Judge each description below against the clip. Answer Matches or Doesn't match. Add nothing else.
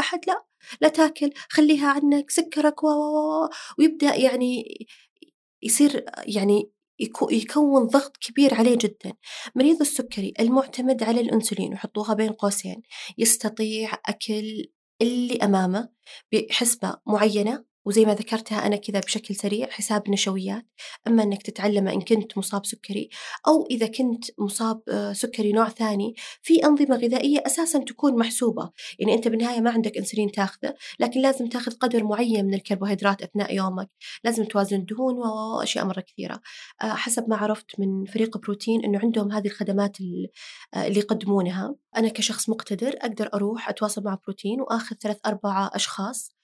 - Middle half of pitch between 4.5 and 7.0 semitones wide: Doesn't match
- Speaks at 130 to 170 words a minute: Matches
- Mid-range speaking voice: Doesn't match